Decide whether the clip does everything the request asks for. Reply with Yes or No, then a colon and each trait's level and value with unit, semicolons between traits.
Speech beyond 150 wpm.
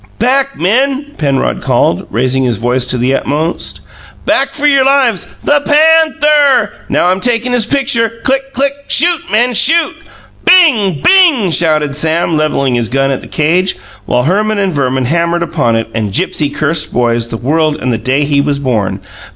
Yes: average, 175 wpm